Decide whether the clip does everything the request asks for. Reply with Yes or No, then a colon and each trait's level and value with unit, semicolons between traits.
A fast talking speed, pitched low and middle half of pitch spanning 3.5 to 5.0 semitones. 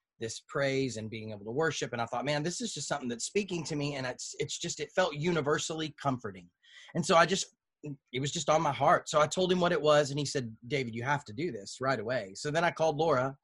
No: fast, 270 wpm; medium, 150 Hz; average, 4.2 semitones